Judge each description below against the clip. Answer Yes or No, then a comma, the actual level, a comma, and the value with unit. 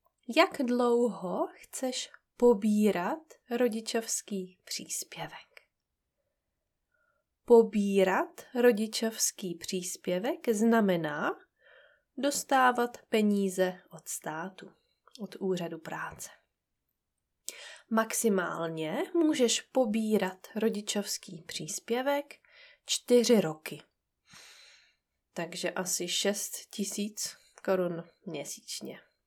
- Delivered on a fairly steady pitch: No, average, 4.8 semitones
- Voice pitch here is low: No, high, 220 Hz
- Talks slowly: Yes, slow, 60 wpm